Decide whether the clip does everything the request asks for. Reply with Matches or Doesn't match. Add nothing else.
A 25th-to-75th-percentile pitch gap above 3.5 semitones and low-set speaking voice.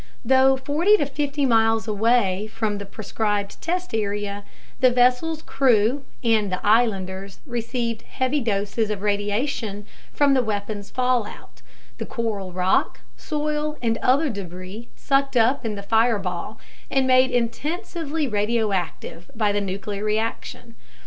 Doesn't match